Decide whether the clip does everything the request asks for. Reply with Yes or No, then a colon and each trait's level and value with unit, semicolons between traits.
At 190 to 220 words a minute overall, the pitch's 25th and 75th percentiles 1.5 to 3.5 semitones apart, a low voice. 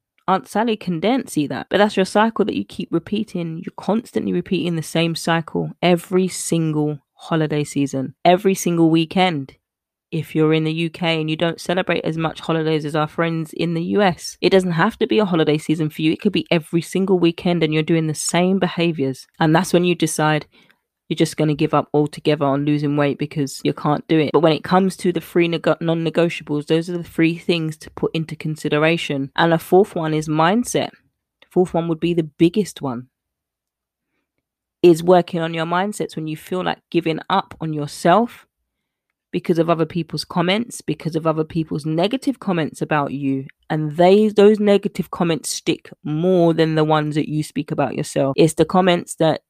No: average, 200 wpm; narrow, 2.6 semitones; medium, 165 Hz